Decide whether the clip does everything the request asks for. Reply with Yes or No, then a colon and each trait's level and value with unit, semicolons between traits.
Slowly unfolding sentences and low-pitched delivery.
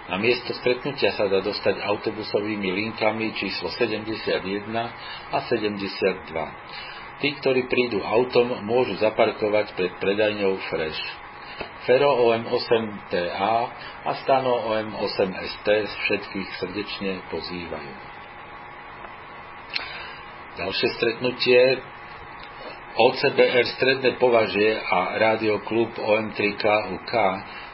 Yes: slow, 80 wpm; low, 110 Hz